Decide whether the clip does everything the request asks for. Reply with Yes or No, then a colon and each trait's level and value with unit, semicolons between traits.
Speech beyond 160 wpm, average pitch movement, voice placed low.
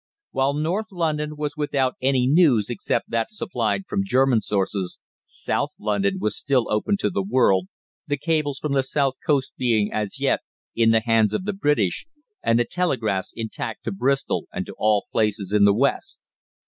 No: average, 175 wpm; wide, 5.7 semitones; low, 130 Hz